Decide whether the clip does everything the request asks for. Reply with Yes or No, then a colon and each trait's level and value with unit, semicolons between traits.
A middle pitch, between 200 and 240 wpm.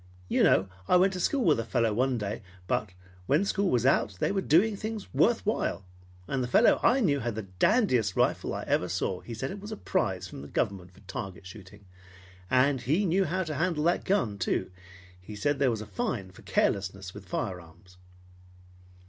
No: low, 120 Hz; fast, 205 wpm